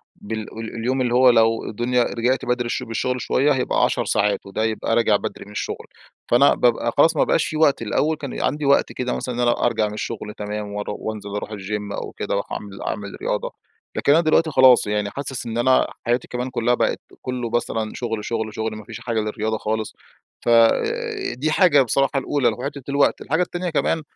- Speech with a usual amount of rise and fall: Yes, average, 3.2 semitones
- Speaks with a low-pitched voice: Yes, low, 120 Hz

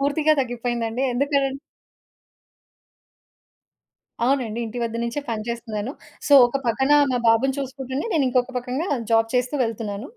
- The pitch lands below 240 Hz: No, high, 245 Hz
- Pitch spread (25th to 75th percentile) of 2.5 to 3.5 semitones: Yes, average, 2.9 semitones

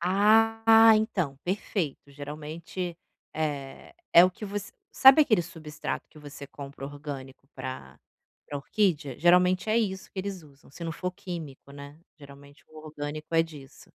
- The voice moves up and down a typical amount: Yes, average, 4.8 semitones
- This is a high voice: No, medium, 160 Hz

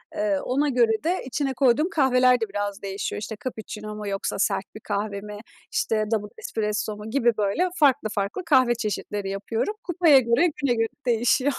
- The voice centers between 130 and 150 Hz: No, high, 225 Hz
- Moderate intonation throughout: Yes, average, 4.2 semitones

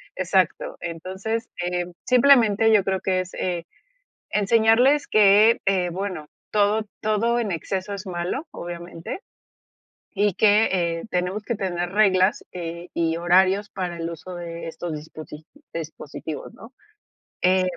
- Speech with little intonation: No, average, 3.4 semitones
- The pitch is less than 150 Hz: No, medium, 185 Hz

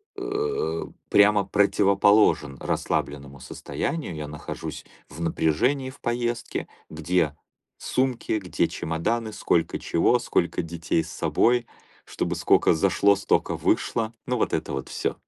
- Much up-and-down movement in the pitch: Yes, wide, 6.8 semitones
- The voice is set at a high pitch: No, low, 100 Hz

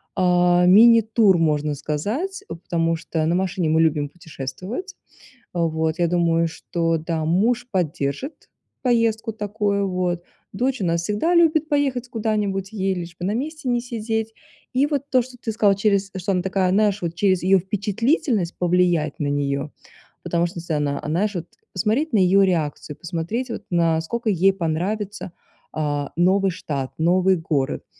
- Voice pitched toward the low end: No, medium, 185 Hz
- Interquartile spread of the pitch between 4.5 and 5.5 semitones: Yes, average, 4.9 semitones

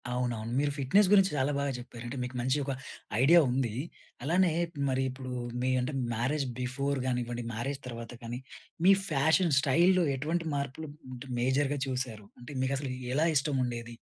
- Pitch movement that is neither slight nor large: Yes, average, 3.0 semitones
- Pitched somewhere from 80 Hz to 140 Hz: Yes, low, 135 Hz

